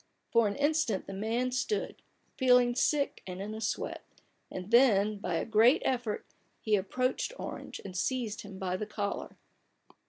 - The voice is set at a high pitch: Yes, high, 220 Hz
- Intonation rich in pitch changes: No, average, 4.0 semitones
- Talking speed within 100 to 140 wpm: No, average, 160 wpm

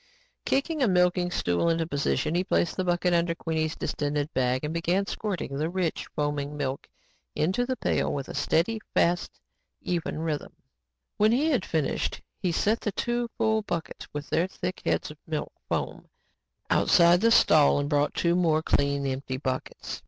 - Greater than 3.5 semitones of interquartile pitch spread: Yes, average, 4.0 semitones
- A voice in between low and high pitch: Yes, medium, 165 Hz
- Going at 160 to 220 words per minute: Yes, average, 175 wpm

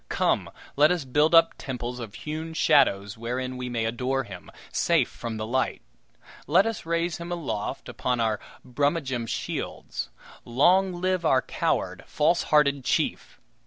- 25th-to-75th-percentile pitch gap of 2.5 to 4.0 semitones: No, wide, 5.5 semitones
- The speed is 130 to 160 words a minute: Yes, average, 145 wpm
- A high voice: No, low, 135 Hz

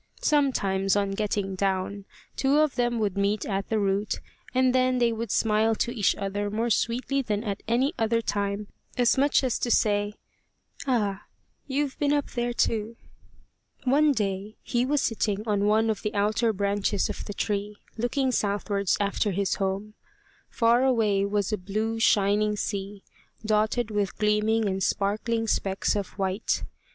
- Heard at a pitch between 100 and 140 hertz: No, high, 210 Hz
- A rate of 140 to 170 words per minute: Yes, average, 160 wpm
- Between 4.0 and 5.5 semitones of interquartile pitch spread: No, average, 2.9 semitones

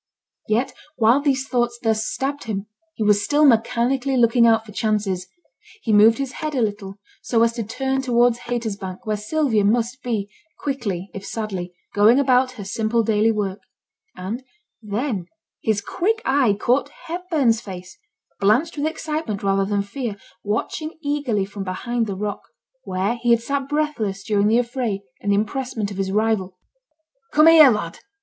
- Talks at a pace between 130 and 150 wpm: No, average, 165 wpm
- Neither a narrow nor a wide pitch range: Yes, average, 4.3 semitones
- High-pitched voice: Yes, high, 225 Hz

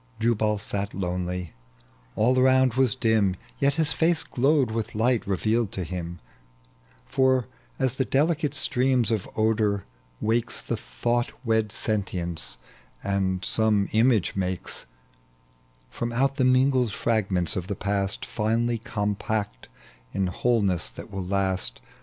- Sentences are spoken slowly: Yes, slow, 130 wpm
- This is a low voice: Yes, low, 110 Hz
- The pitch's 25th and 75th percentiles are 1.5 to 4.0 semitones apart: No, average, 4.4 semitones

